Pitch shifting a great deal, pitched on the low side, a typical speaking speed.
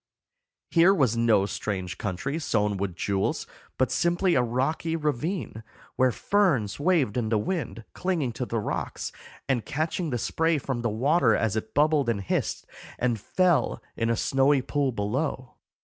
Yes: wide, 6.1 semitones; low, 130 Hz; average, 160 wpm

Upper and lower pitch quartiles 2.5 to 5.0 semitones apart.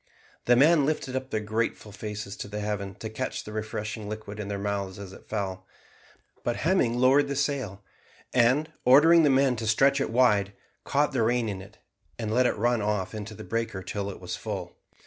Yes: average, 4.1 semitones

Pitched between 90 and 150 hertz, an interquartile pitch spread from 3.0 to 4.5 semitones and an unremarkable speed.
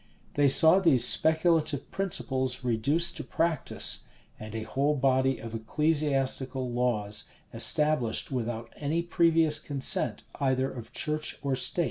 No: low, 135 Hz; average, 3.7 semitones; slow, 125 wpm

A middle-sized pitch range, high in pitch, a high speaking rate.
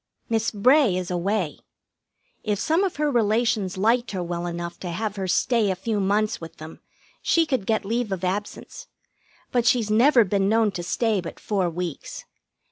No: average, 4.2 semitones; high, 210 Hz; average, 180 wpm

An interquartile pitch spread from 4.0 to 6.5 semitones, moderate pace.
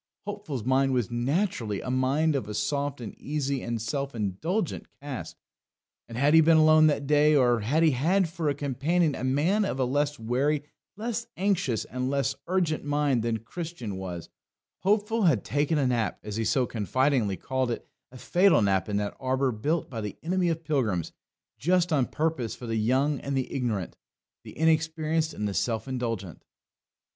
Yes: average, 5.0 semitones; average, 180 wpm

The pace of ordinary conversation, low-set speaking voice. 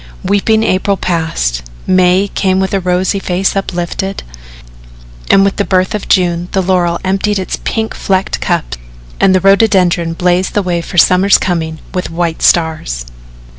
No: average, 155 wpm; medium, 185 Hz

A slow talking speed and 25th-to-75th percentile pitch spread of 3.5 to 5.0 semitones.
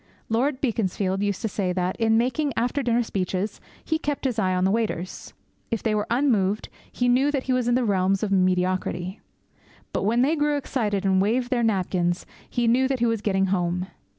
No: fast, 205 wpm; average, 4.6 semitones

